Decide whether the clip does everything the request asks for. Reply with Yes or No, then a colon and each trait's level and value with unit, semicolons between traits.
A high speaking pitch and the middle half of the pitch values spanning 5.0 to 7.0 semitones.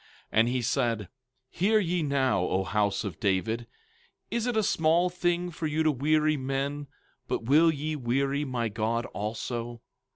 No: low, 135 Hz; wide, 5.4 semitones